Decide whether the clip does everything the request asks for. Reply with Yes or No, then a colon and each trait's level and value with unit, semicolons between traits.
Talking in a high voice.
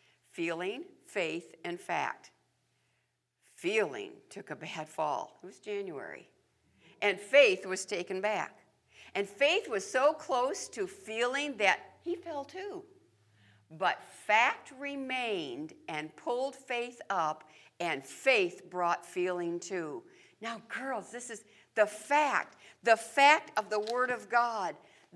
Yes: high, 240 Hz